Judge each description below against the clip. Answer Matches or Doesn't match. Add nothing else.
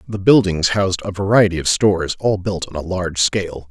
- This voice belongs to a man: Matches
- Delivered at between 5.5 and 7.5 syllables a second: Matches